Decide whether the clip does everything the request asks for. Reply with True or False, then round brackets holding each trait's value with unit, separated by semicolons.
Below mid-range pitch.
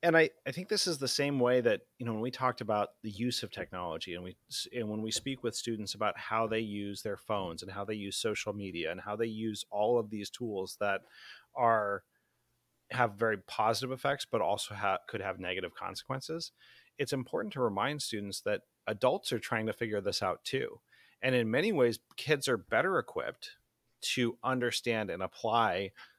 True (115 Hz)